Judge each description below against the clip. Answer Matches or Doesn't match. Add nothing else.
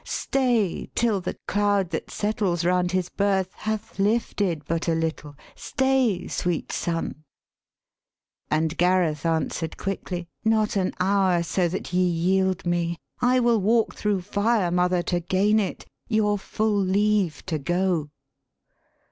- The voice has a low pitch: Doesn't match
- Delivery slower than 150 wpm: Matches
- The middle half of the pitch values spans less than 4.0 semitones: Matches